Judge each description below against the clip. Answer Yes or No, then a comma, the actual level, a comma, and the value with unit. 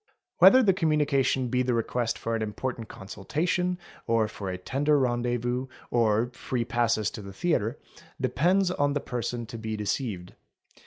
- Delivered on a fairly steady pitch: No, average, 4.5 semitones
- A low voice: Yes, low, 120 Hz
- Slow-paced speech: No, average, 160 wpm